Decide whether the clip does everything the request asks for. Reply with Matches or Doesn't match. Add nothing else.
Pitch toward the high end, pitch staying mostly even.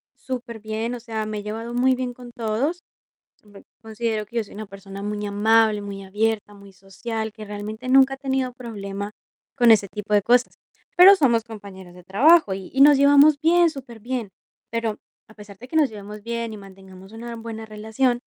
Doesn't match